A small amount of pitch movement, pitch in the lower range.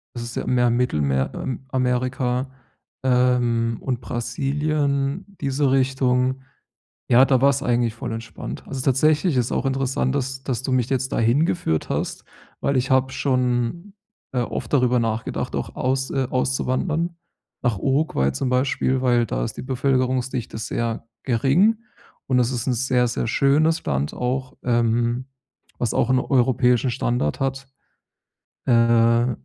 Yes: narrow, 2.1 semitones; low, 125 Hz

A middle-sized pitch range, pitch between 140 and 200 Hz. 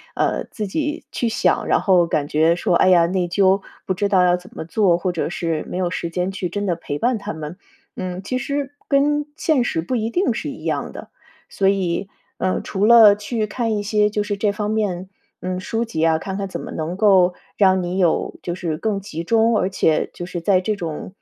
Yes: average, 3.3 semitones; high, 190 Hz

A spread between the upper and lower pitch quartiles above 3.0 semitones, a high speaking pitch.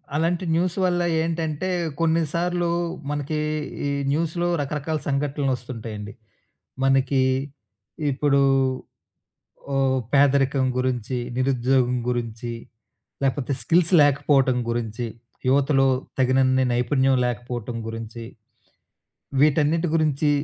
No: average, 3.5 semitones; low, 135 Hz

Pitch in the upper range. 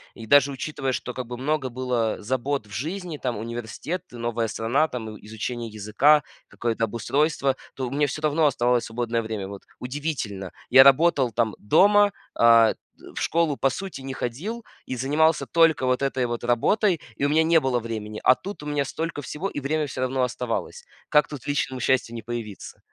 No: low, 130 Hz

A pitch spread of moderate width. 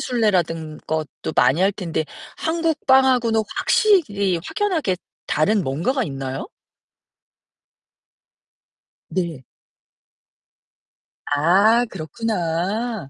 No: wide, 7.2 semitones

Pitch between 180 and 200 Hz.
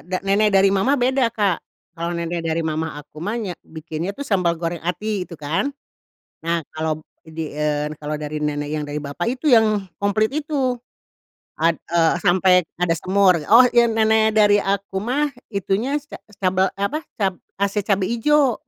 Yes: high, 190 Hz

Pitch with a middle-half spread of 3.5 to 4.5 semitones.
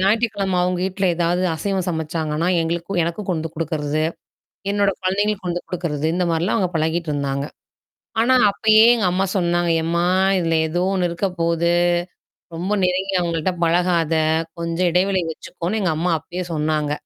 No: narrow, 2.5 semitones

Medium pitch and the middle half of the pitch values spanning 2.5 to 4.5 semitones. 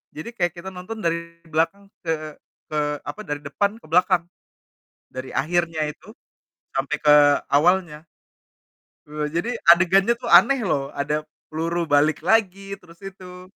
Yes: medium, 170 Hz; average, 3.8 semitones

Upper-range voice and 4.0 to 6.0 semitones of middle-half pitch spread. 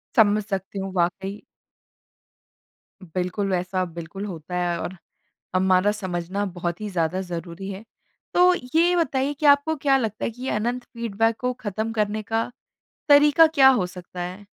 Yes: high, 205 Hz; average, 5.1 semitones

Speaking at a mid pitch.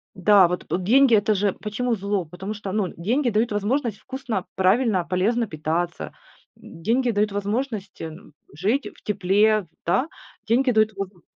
No: high, 205 Hz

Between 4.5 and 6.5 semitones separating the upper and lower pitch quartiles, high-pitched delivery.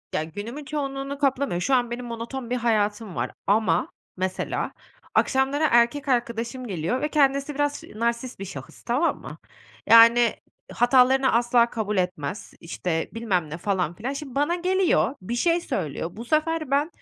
Yes: average, 5.1 semitones; high, 240 Hz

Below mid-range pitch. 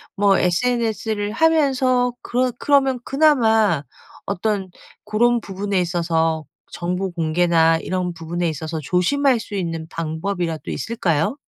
No: high, 195 Hz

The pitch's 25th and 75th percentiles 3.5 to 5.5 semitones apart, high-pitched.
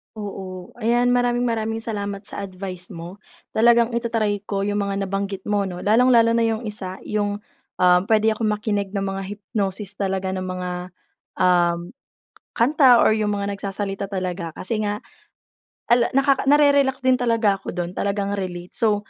No: average, 3.1 semitones; high, 205 Hz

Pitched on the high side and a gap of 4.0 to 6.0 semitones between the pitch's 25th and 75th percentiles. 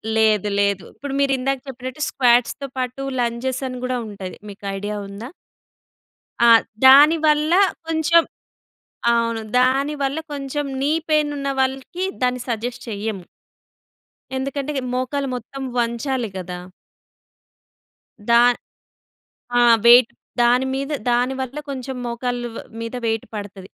No: very high, 255 Hz; average, 3.0 semitones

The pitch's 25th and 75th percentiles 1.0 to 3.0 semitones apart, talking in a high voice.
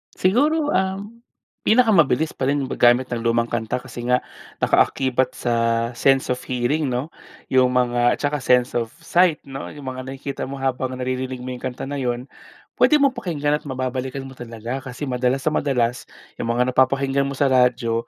No: narrow, 2.4 semitones; low, 130 Hz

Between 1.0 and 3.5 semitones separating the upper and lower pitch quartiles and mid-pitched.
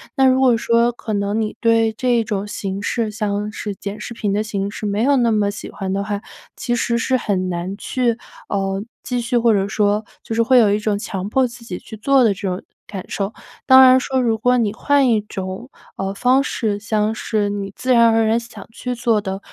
No: average, 3.0 semitones; high, 220 Hz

